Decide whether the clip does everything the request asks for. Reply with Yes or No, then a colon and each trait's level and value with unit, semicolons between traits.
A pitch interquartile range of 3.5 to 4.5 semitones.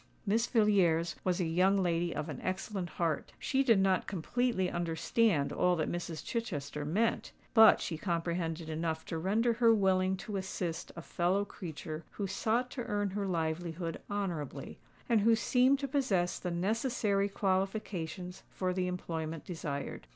Yes: average, 3.9 semitones